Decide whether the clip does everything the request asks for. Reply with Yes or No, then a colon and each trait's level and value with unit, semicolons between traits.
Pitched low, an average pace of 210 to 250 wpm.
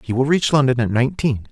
Yes: low, 130 Hz; fast, 240 wpm